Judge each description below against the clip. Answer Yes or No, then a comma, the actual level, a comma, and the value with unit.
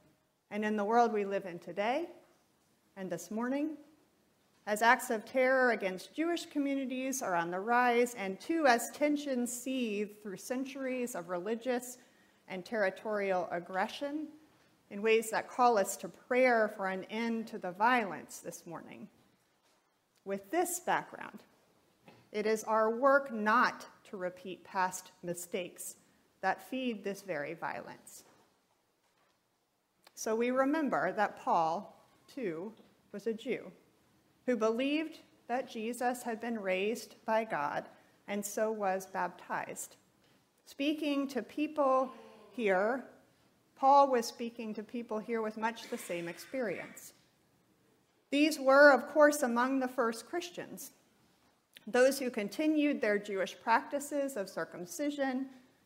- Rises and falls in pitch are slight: No, average, 4.8 semitones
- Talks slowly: Yes, slow, 130 wpm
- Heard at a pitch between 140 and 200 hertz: No, high, 230 Hz